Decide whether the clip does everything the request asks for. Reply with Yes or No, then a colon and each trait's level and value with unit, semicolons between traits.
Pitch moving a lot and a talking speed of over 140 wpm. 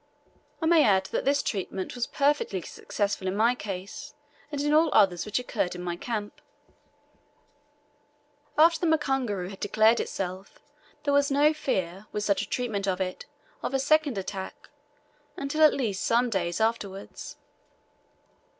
Yes: wide, 6.6 semitones; average, 150 wpm